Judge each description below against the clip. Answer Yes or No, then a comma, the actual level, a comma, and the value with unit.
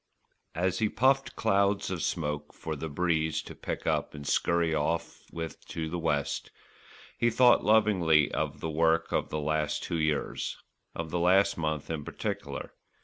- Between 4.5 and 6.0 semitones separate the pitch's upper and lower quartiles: No, average, 3.6 semitones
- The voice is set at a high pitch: No, very low, 80 Hz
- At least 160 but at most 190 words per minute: Yes, average, 165 wpm